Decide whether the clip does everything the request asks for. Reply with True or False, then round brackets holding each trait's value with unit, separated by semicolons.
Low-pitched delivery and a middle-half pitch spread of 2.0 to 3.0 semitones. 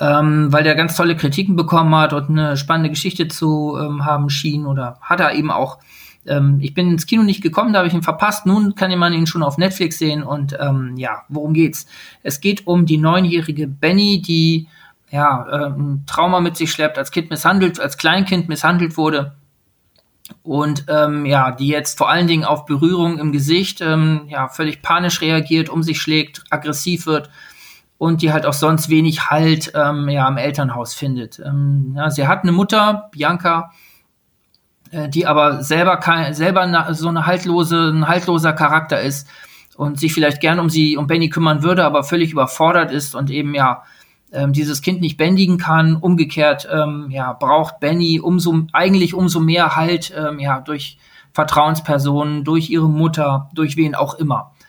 False (155 Hz; 2.5 semitones)